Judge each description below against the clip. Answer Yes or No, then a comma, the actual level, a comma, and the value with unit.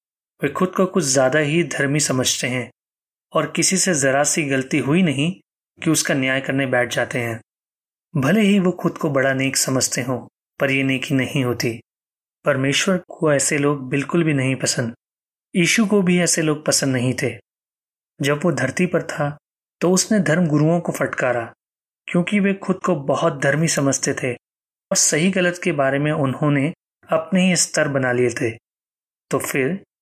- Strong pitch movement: No, average, 4.7 semitones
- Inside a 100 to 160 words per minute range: No, average, 175 wpm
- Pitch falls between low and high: Yes, medium, 150 Hz